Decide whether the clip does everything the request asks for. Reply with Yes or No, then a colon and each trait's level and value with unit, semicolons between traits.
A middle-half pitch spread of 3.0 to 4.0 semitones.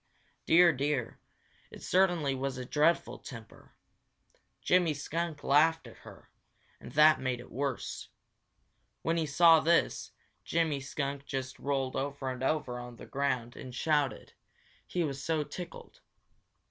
Yes: average, 3.5 semitones